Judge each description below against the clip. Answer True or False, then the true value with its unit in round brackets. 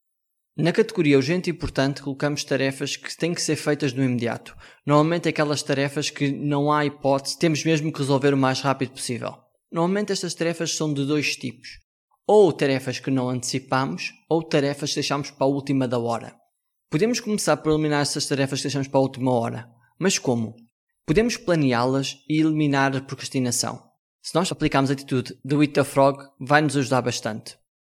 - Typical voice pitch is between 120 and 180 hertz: True (140 Hz)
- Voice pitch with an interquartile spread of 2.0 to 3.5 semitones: True (2.6 semitones)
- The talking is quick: False (175 wpm)